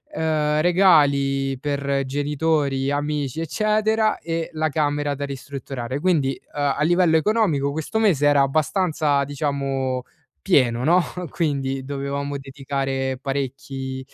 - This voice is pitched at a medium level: Yes, medium, 145 Hz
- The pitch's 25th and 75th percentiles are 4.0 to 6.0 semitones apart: No, narrow, 2.6 semitones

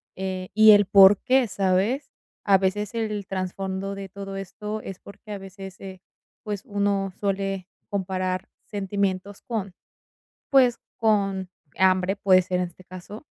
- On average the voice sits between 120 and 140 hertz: No, high, 195 Hz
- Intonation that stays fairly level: Yes, narrow, 1.6 semitones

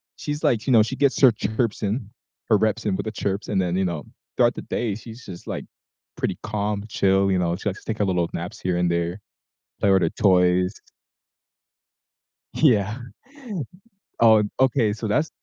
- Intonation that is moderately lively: Yes, average, 3.2 semitones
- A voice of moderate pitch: No, low, 105 Hz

